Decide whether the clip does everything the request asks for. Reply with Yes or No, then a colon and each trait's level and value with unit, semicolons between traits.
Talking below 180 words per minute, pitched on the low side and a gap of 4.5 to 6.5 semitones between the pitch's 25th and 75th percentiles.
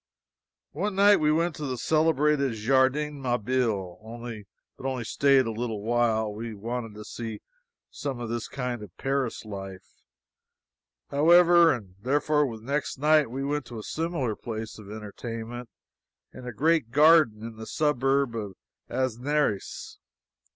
Yes: average, 145 wpm; low, 125 Hz; average, 4.8 semitones